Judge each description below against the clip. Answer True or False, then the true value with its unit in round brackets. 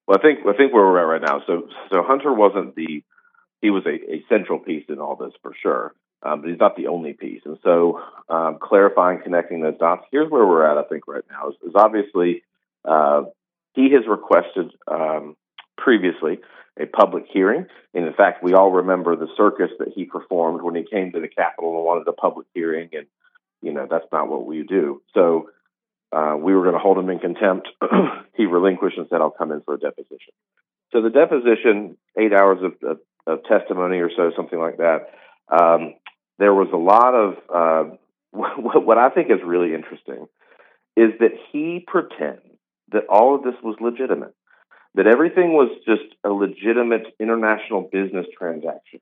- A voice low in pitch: True (100 Hz)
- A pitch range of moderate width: False (6.7 semitones)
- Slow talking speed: False (190 wpm)